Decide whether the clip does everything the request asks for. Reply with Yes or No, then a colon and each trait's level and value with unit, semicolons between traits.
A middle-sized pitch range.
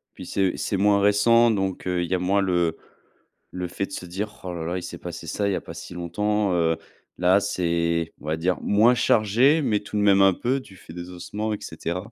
Yes: average, 3.0 semitones